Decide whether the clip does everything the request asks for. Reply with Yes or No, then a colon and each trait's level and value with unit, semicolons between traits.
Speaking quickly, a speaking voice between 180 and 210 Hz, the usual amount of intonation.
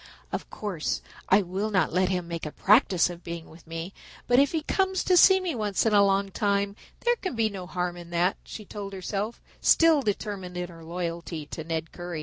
Yes: fast, 215 wpm; high, 190 Hz; average, 3.7 semitones